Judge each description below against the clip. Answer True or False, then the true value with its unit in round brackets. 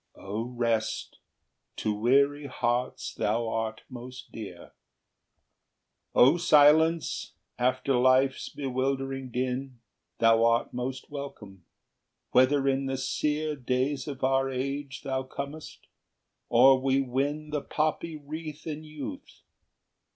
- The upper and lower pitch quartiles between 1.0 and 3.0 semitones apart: True (2.6 semitones)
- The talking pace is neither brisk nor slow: False (115 wpm)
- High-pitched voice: False (135 Hz)